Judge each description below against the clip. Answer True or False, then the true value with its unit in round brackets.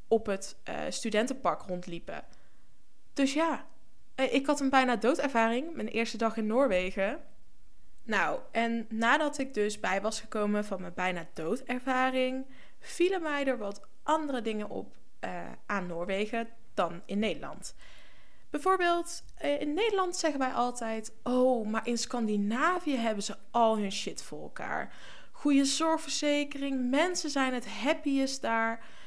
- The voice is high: True (245 Hz)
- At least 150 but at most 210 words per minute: False (140 wpm)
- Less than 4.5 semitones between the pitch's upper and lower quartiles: False (4.8 semitones)